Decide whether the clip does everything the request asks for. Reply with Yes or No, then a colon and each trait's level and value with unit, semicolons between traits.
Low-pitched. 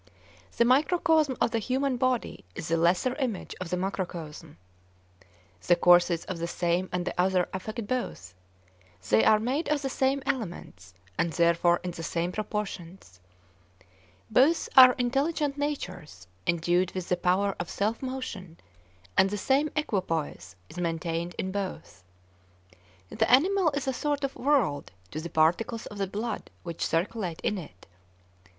No: high, 190 Hz